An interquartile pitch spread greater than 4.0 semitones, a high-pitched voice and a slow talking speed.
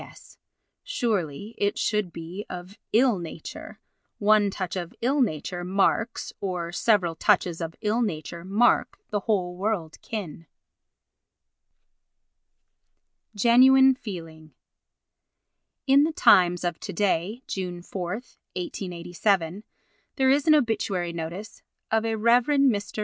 Yes: average, 4.5 semitones; high, 195 Hz; slow, 110 wpm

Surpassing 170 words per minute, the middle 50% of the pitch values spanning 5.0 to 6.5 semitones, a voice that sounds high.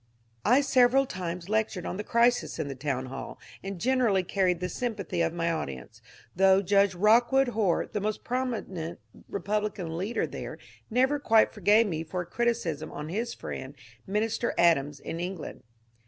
No: average, 165 wpm; wide, 5.4 semitones; high, 195 Hz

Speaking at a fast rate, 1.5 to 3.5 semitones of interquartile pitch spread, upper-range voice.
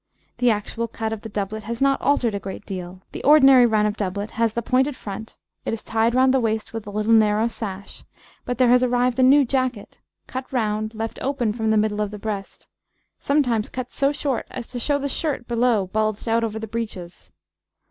Yes: fast, 215 wpm; average, 3.1 semitones; high, 225 Hz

